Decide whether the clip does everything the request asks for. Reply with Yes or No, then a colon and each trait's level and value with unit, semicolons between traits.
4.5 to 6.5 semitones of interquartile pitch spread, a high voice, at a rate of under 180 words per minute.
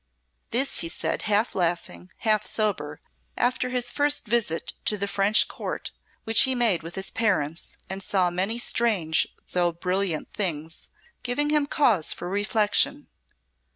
Yes: average, 5.3 semitones; high, 205 Hz; average, 145 wpm